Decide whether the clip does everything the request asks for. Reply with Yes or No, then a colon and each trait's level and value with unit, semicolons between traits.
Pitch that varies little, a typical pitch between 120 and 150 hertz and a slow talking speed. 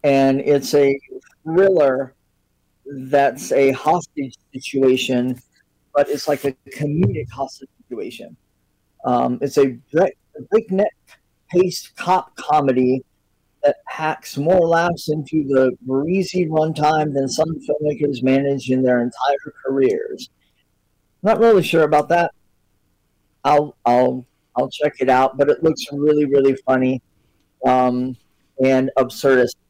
No: average, 3.0 semitones; medium, 140 Hz; slow, 115 wpm